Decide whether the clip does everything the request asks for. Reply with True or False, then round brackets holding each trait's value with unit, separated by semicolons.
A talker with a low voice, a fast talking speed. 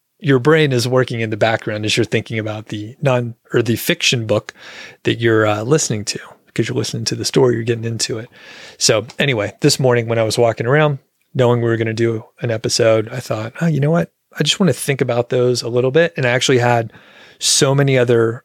True (120 Hz; 235 wpm)